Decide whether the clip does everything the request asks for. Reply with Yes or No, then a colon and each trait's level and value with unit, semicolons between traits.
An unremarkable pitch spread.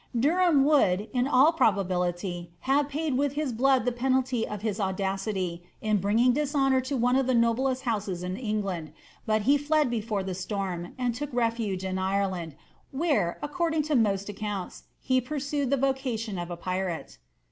No: wide, 5.9 semitones